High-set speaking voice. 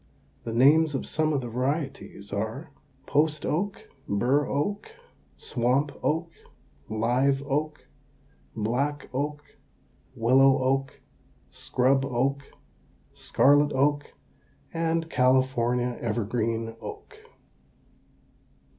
No: low, 135 Hz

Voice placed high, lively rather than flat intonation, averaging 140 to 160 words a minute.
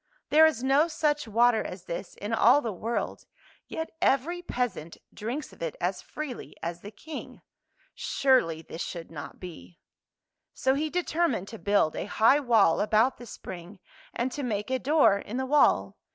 No: high, 235 Hz; wide, 6.4 semitones; average, 175 wpm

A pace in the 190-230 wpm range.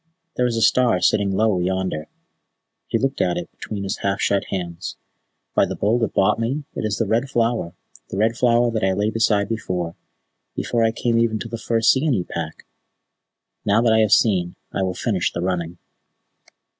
Yes: average, 195 wpm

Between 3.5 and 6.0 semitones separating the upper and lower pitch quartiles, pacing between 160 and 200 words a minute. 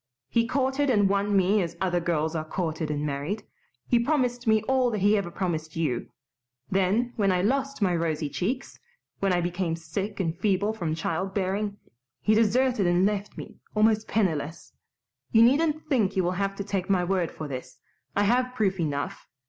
Yes: average, 4.3 semitones; average, 185 wpm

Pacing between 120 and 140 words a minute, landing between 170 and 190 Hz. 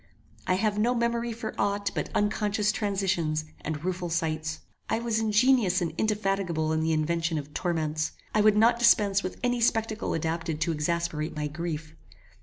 No: average, 165 wpm; medium, 185 Hz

